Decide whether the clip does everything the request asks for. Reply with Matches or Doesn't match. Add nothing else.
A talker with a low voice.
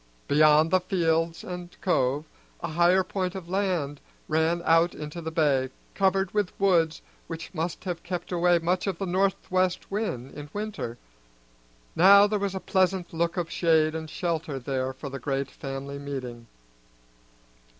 Doesn't match